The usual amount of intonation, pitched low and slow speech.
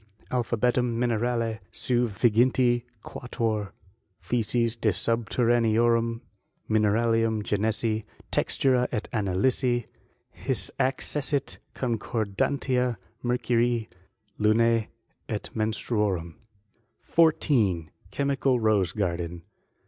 No: narrow, 2.3 semitones; low, 115 Hz; slow, 70 wpm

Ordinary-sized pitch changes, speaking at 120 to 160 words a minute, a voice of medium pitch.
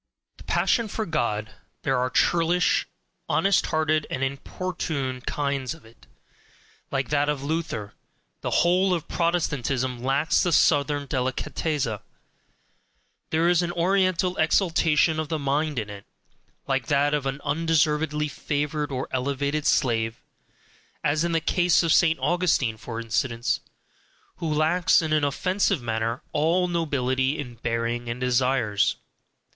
Yes: average, 4.2 semitones; slow, 135 wpm; medium, 145 Hz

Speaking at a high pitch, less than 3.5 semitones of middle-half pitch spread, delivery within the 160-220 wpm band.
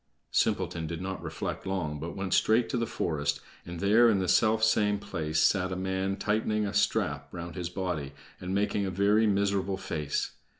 No: very low, 95 Hz; average, 3.1 semitones; average, 185 wpm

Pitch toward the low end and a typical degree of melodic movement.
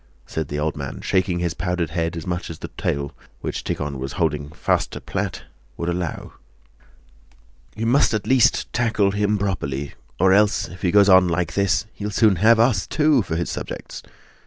Yes: very low, 90 Hz; average, 4.2 semitones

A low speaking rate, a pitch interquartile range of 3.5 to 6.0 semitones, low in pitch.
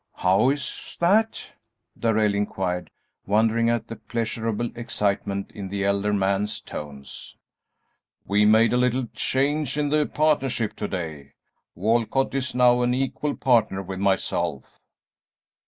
Yes: slow, 125 wpm; average, 4.3 semitones; low, 110 Hz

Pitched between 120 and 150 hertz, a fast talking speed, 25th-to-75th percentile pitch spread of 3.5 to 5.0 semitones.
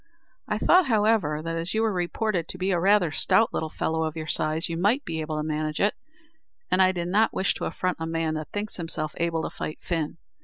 No: medium, 170 Hz; fast, 235 wpm; average, 3.9 semitones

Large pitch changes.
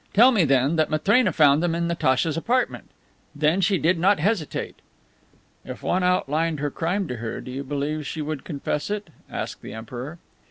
No: average, 4.2 semitones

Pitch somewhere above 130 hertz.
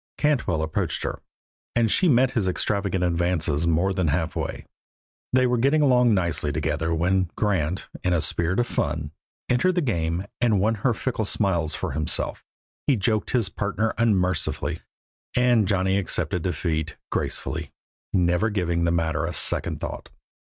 No: very low, 95 Hz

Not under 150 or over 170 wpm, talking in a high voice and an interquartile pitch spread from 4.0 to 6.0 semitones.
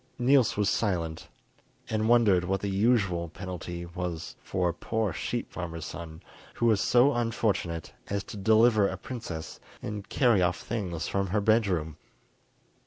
No: average, 155 wpm; low, 100 Hz; average, 4.3 semitones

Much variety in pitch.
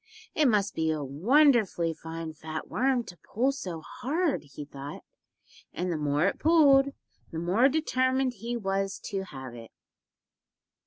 Yes: wide, 8.6 semitones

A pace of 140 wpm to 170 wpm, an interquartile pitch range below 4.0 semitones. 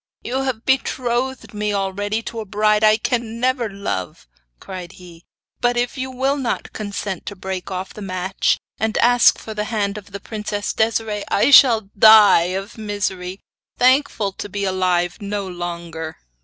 Yes: average, 165 wpm; average, 3.4 semitones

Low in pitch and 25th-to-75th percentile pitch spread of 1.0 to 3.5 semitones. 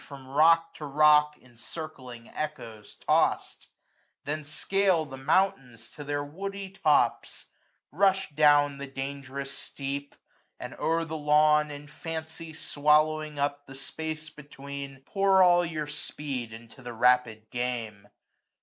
No: medium, 145 Hz; average, 2.7 semitones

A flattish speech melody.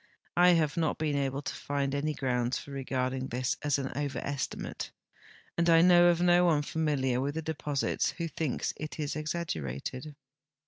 No: average, 3.3 semitones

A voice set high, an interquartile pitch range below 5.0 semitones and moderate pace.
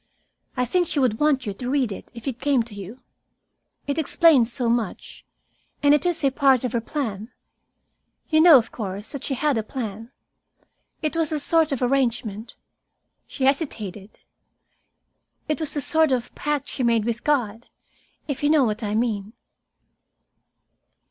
Yes: very high, 255 Hz; average, 4.6 semitones; average, 170 wpm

